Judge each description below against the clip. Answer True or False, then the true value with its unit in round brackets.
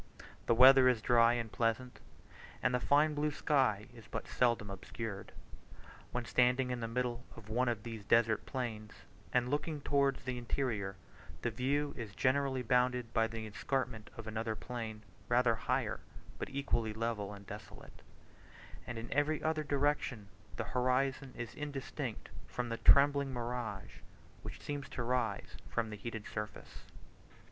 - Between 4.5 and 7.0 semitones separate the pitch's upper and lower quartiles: False (3.0 semitones)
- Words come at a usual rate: True (155 wpm)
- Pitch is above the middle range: False (120 Hz)